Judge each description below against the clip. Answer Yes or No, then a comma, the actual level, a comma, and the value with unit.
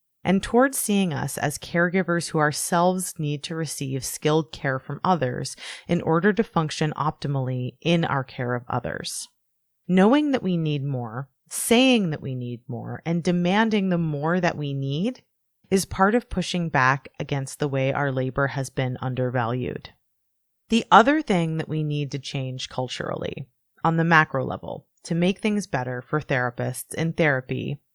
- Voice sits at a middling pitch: Yes, medium, 150 Hz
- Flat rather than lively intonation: No, average, 4.9 semitones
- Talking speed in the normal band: Yes, average, 165 wpm